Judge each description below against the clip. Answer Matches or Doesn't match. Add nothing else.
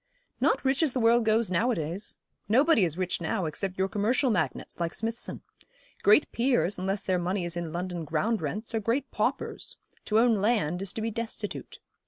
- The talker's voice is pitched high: Matches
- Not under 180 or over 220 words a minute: Matches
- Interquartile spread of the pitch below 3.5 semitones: Doesn't match